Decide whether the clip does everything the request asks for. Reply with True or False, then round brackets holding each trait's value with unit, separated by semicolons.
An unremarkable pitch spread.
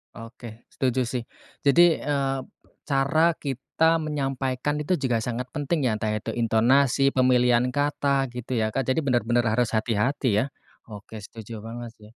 True (3.2 semitones)